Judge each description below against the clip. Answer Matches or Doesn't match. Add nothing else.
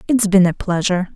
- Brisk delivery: Matches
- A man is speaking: Doesn't match